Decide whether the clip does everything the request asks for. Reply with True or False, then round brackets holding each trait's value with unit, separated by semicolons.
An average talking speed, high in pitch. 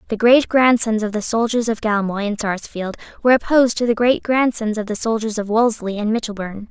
True (190 wpm; 220 Hz)